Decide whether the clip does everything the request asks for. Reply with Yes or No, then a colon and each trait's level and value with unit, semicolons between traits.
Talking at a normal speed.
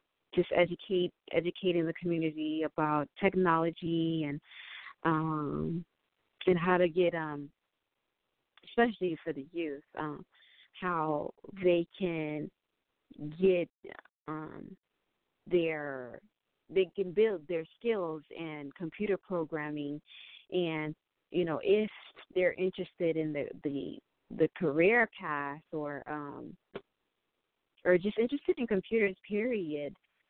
No: slow, 105 wpm